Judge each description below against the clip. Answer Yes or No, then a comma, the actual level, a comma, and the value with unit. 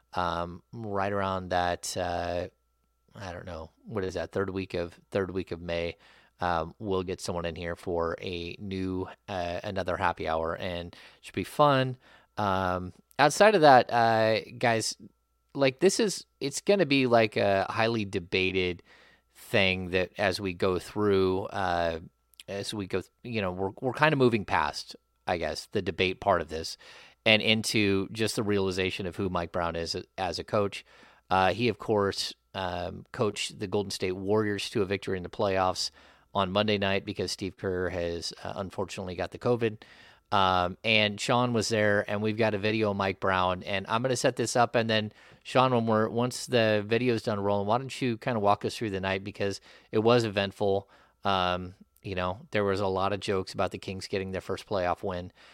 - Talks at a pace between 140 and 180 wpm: No, average, 195 wpm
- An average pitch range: Yes, average, 3.4 semitones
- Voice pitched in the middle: No, low, 100 Hz